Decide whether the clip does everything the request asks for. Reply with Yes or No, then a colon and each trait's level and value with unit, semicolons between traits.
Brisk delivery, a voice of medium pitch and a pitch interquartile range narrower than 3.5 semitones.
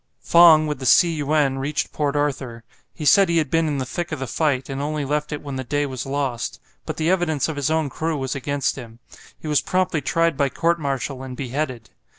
Yes: fast, 230 wpm; medium, 145 Hz; average, 2.8 semitones